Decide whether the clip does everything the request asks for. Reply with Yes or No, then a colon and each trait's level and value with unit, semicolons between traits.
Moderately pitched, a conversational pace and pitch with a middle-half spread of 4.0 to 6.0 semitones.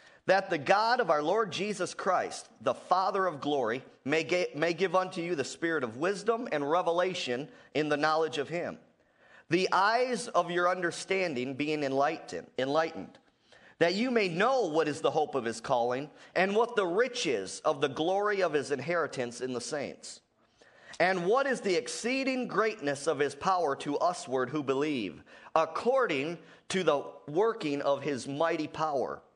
Yes: medium, 165 Hz; average, 165 wpm; average, 4.6 semitones